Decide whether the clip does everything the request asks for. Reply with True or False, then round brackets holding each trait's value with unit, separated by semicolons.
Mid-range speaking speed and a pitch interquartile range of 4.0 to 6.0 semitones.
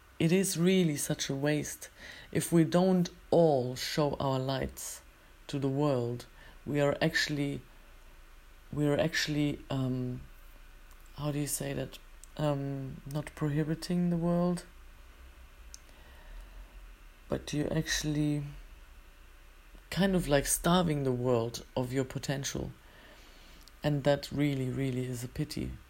False (120 wpm; 4.3 semitones)